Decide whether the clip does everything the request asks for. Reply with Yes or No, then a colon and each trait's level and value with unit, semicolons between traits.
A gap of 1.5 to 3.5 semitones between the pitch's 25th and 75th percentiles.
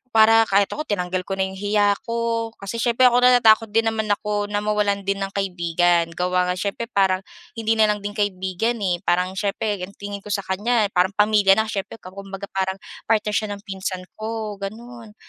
Yes: narrow, 2.4 semitones